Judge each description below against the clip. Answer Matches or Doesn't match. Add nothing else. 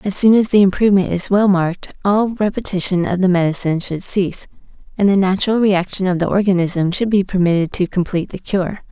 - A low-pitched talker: Doesn't match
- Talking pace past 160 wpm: Matches